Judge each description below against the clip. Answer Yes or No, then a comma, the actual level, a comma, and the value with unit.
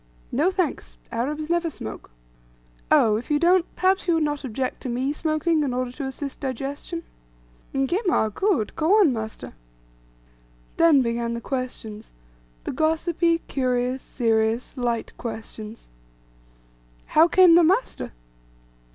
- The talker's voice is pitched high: Yes, very high, 280 Hz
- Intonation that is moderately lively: No, wide, 5.7 semitones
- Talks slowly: Yes, slow, 130 wpm